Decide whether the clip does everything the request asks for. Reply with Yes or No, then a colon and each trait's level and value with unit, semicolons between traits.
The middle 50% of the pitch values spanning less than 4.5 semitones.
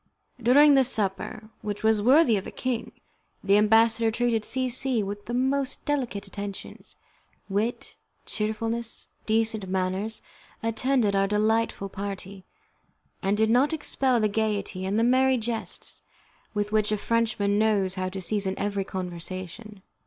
Yes: average, 2.8 semitones